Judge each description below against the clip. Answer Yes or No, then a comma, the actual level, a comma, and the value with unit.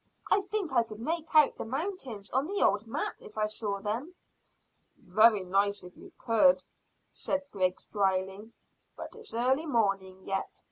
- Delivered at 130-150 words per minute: No, average, 160 wpm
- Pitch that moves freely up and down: Yes, wide, 6.2 semitones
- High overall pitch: Yes, high, 225 Hz